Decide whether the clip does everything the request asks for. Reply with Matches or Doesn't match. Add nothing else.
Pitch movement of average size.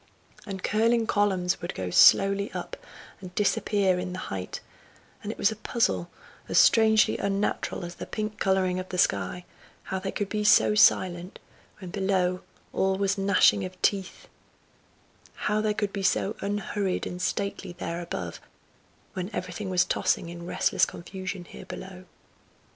Doesn't match